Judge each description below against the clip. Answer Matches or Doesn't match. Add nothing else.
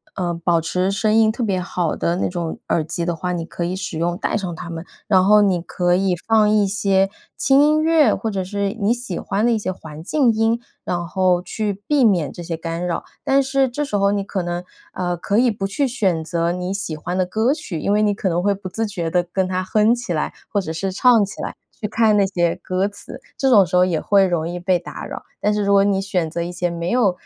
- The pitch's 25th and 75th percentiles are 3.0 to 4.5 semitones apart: Matches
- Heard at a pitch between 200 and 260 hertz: Doesn't match